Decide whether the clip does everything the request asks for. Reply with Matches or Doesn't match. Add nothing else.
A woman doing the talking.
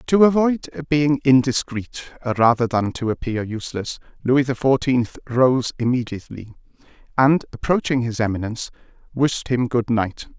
Doesn't match